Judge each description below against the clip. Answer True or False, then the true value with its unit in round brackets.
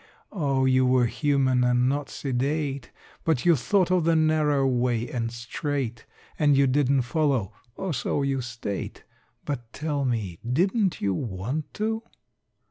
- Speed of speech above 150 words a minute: False (145 wpm)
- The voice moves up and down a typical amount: True (3.7 semitones)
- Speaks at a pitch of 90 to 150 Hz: True (135 Hz)